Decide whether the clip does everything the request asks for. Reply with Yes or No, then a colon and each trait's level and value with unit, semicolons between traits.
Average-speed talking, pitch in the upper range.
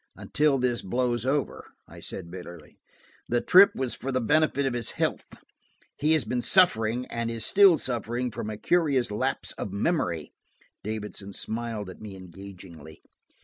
No: average, 155 wpm; low, 120 Hz